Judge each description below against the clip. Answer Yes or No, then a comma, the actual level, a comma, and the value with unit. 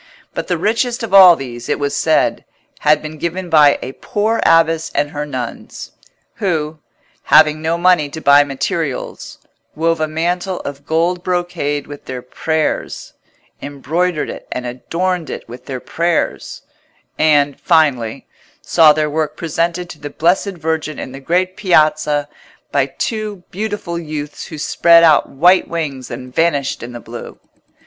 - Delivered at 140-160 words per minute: Yes, average, 155 wpm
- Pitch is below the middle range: No, medium, 155 Hz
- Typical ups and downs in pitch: Yes, average, 3.2 semitones